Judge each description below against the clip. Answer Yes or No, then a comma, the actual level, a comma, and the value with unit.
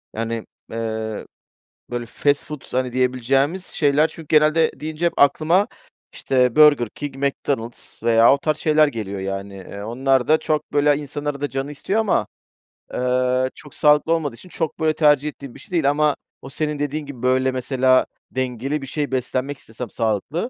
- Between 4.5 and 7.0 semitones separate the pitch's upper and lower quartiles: No, average, 3.3 semitones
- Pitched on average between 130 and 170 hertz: Yes, medium, 140 Hz